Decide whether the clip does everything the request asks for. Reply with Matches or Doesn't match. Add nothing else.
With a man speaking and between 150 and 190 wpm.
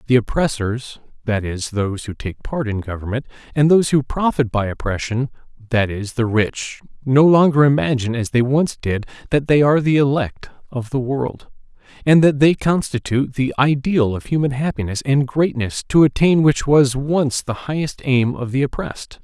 Matches